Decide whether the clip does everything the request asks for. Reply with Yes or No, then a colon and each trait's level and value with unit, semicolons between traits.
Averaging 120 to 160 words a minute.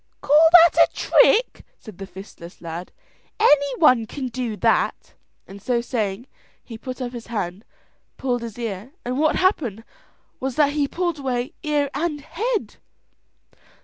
Yes: average, 150 wpm